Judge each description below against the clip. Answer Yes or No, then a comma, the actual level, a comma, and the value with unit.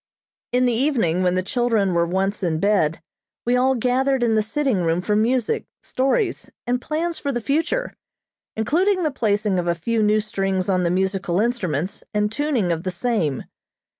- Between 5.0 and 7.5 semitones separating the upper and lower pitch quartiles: Yes, wide, 5.6 semitones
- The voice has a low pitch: No, high, 215 Hz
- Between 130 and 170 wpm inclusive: No, average, 180 wpm